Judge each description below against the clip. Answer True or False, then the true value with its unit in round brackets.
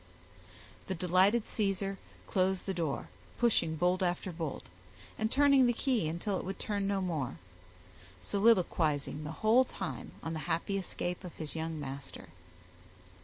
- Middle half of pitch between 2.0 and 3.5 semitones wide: False (3.9 semitones)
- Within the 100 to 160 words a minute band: True (145 wpm)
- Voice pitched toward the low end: False (185 Hz)